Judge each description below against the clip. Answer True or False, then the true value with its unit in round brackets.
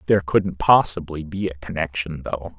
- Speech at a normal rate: True (160 wpm)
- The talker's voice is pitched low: True (85 Hz)